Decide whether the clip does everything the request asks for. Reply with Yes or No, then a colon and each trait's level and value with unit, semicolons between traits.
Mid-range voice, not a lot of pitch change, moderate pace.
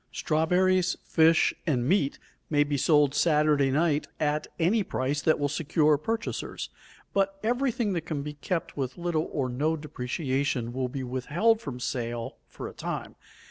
No: medium, 150 Hz; average, 4.0 semitones; average, 160 wpm